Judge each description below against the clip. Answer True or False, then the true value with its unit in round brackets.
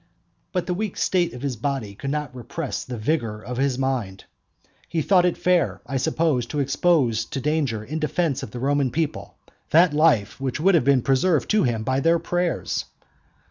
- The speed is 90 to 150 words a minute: False (185 wpm)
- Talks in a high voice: False (140 Hz)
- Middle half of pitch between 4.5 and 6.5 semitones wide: True (5.0 semitones)